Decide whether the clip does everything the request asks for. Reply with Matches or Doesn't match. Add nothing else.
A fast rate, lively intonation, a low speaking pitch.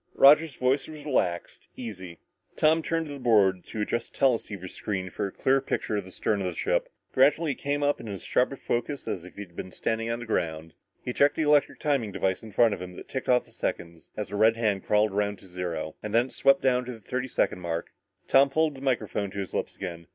Matches